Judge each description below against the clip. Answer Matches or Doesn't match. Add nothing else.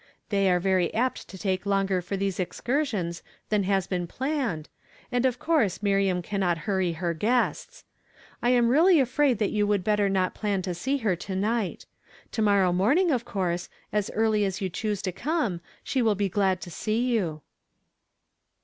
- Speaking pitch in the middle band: Doesn't match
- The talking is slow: Doesn't match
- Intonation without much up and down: Doesn't match